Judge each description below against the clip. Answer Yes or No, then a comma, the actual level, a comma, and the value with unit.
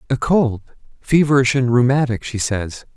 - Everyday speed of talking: No, slow, 120 wpm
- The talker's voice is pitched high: No, low, 125 Hz